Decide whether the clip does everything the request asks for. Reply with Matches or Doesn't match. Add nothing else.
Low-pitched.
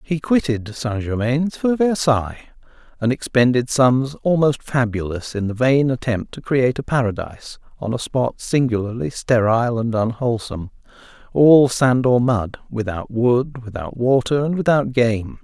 Matches